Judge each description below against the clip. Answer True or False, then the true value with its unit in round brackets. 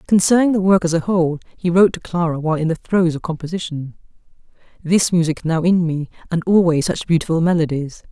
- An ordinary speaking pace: True (190 wpm)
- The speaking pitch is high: False (170 Hz)